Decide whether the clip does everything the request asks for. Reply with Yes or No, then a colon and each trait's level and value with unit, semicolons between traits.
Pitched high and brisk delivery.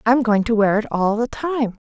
Yes: high, 225 Hz; fast, 255 wpm